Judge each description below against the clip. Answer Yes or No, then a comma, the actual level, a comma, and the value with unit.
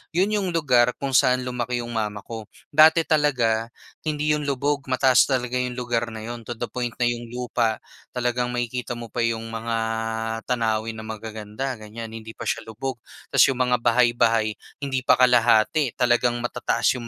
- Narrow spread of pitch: Yes, narrow, 2.1 semitones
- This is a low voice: Yes, low, 120 Hz